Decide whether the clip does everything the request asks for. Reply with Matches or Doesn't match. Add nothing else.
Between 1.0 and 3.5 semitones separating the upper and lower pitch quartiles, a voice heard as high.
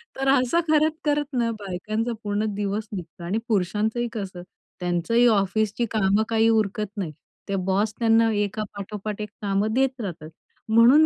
Matches